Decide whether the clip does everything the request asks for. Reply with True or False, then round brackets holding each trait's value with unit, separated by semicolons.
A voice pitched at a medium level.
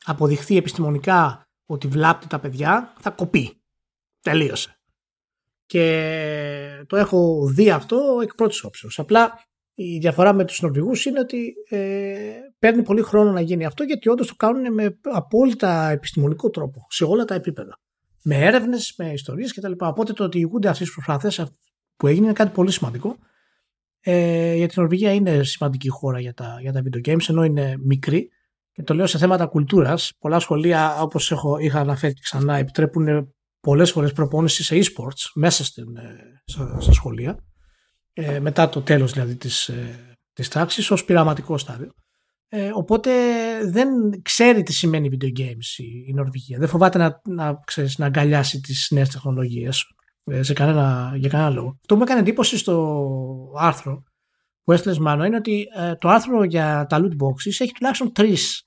True (165 Hz)